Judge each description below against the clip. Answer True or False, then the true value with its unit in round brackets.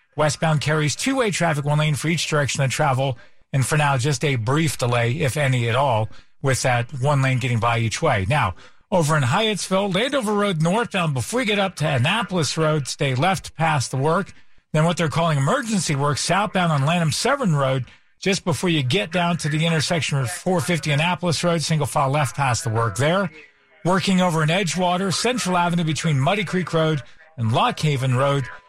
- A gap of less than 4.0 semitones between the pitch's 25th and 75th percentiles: False (4.4 semitones)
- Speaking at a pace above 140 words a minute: True (190 wpm)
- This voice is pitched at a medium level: True (155 Hz)